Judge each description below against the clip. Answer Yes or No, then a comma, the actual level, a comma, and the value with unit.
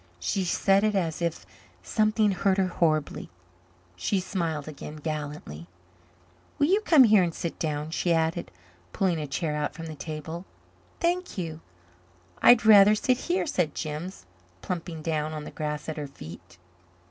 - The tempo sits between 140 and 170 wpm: Yes, average, 160 wpm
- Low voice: No, medium, 165 Hz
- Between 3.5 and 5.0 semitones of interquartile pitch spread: Yes, average, 4.4 semitones